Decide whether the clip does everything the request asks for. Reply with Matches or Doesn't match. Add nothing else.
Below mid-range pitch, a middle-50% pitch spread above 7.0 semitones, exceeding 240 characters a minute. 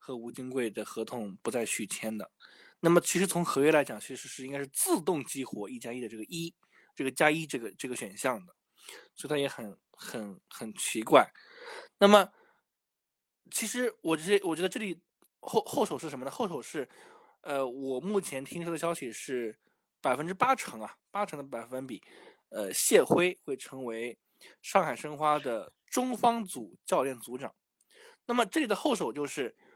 Doesn't match